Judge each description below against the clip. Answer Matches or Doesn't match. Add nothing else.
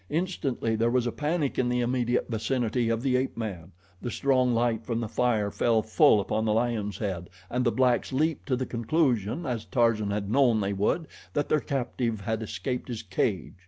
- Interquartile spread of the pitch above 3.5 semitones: Doesn't match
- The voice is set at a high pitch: Doesn't match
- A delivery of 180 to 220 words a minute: Matches